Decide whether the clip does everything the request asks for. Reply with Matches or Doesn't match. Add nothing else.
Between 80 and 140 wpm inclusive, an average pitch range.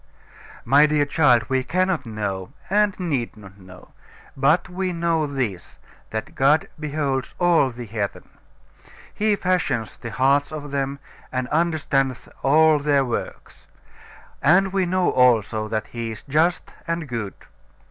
Doesn't match